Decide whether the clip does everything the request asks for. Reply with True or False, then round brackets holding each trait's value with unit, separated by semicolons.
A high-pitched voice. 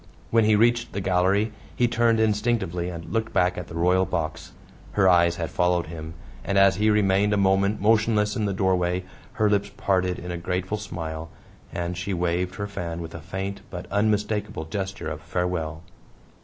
False (95 Hz)